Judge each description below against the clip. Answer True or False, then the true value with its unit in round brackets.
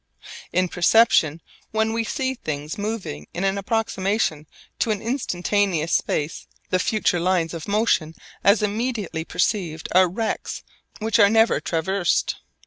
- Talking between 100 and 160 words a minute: True (135 wpm)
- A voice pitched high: True (195 Hz)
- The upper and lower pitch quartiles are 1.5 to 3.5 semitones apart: False (4.7 semitones)